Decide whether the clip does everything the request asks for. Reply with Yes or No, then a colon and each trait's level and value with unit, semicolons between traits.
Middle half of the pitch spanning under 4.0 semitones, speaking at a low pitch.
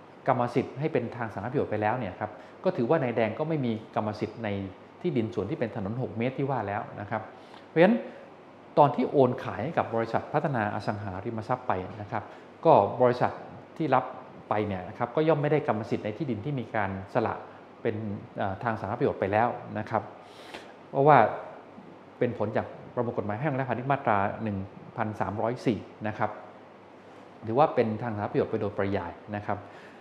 Yes: average, 2.8 semitones; low, 110 Hz